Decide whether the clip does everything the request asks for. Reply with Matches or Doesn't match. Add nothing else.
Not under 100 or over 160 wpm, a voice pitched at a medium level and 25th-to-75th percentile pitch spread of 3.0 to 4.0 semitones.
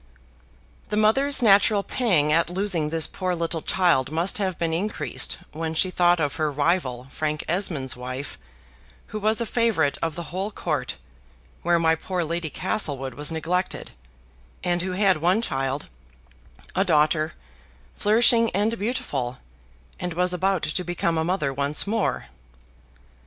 Doesn't match